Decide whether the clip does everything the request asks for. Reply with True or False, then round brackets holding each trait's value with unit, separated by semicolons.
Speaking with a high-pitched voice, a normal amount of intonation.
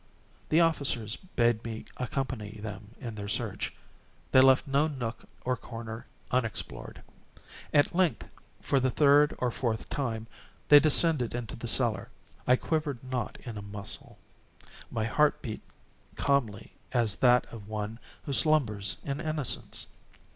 False (125 Hz; 4.2 semitones)